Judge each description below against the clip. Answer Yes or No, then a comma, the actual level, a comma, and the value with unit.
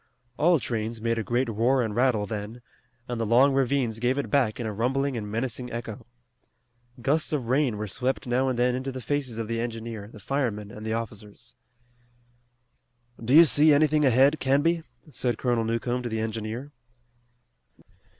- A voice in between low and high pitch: No, low, 120 Hz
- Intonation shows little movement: No, average, 3.1 semitones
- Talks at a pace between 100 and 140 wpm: No, average, 175 wpm